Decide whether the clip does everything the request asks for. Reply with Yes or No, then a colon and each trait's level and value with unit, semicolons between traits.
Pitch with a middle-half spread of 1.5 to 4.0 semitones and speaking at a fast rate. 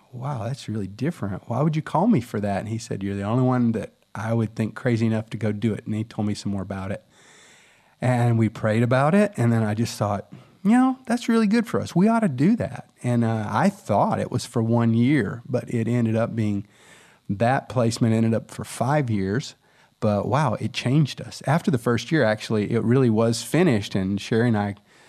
No: average, 4.8 semitones; fast, 230 wpm